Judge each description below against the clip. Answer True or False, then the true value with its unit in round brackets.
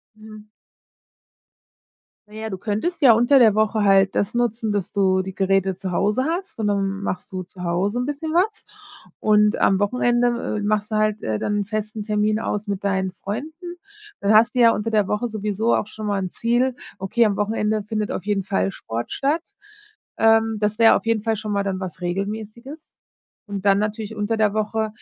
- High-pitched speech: True (215 Hz)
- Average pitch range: False (2.3 semitones)